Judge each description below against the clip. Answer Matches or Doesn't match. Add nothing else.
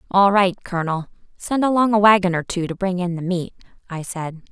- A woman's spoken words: Matches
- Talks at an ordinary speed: Doesn't match